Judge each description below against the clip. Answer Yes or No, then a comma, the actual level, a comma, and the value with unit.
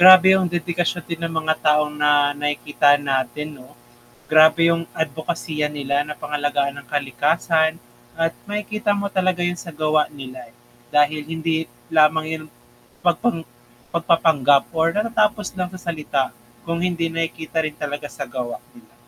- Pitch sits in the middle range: Yes, medium, 160 Hz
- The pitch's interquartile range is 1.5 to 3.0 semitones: Yes, average, 2.7 semitones